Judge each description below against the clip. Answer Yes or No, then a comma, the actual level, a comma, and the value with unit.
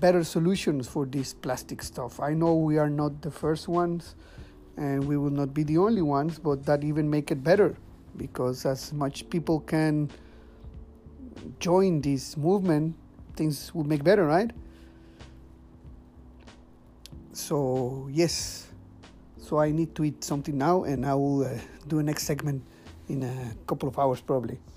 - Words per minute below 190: Yes, average, 155 wpm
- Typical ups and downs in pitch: Yes, average, 3.5 semitones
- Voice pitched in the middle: Yes, medium, 145 Hz